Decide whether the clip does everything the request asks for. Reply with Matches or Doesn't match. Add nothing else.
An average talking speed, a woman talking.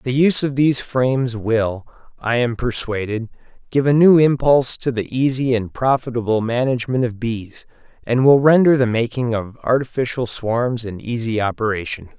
Doesn't match